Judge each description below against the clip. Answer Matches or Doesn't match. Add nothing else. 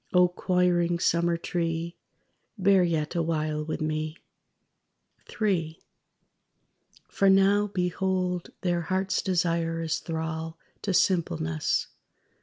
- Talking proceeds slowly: Matches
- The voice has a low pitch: Doesn't match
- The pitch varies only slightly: Matches